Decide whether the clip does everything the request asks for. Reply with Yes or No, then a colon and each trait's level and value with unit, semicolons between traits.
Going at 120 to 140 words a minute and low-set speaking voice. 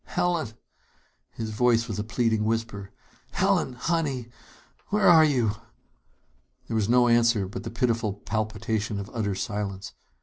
Yes: slow, 135 wpm; low, 115 Hz